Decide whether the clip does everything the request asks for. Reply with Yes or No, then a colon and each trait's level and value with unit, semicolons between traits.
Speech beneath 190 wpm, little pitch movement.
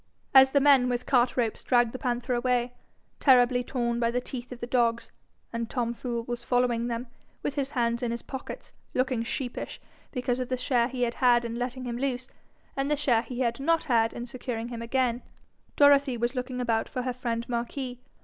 No: fast, 205 wpm; narrow, 1.5 semitones